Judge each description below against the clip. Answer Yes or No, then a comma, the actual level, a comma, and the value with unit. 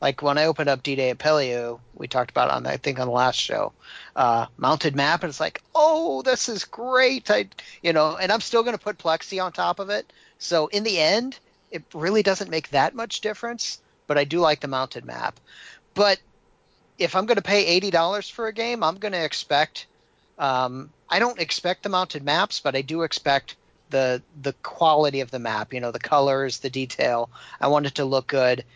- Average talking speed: No, fast, 215 wpm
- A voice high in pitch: No, medium, 155 Hz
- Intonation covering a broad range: Yes, wide, 7.0 semitones